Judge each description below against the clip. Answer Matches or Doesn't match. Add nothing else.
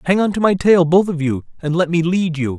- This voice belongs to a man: Matches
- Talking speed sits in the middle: Doesn't match